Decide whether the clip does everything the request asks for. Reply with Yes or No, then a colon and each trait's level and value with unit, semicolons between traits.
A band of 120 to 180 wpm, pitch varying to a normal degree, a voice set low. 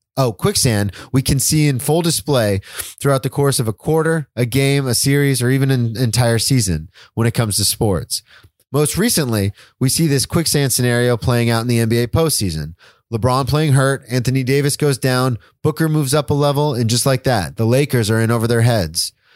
No: average, 200 wpm; average, 3.6 semitones; low, 130 Hz